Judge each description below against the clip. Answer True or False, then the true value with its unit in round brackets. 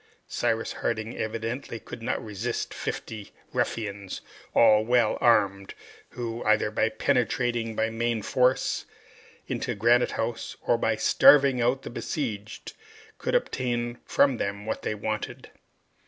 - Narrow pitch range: True (1.9 semitones)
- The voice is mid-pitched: False (115 Hz)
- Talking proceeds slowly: True (125 wpm)